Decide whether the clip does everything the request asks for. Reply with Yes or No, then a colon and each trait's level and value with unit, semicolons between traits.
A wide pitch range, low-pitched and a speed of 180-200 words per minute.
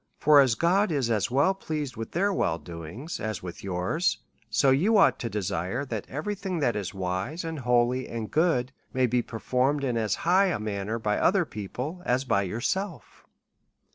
Yes: wide, 7.0 semitones; low, 125 Hz; average, 190 wpm